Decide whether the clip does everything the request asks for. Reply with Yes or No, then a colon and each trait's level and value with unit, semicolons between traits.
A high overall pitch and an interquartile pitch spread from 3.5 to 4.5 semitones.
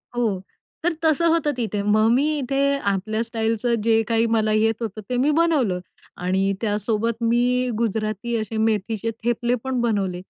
No: high, 225 Hz; narrow, 2.5 semitones